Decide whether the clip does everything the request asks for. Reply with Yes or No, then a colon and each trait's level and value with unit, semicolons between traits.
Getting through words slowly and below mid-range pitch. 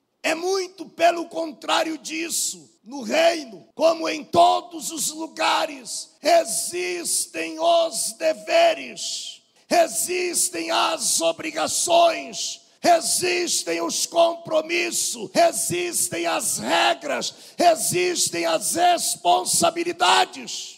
No: slow, 80 wpm; very high, 330 Hz